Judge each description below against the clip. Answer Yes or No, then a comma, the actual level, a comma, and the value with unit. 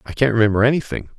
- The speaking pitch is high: No, low, 120 Hz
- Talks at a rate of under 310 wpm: Yes, average, 200 wpm